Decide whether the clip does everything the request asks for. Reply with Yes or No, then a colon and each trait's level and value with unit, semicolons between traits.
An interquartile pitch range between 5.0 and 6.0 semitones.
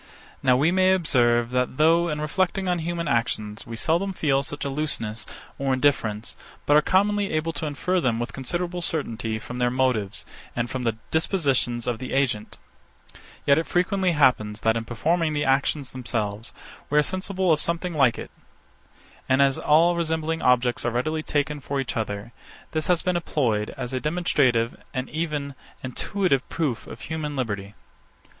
Yes: average, 5.3 semitones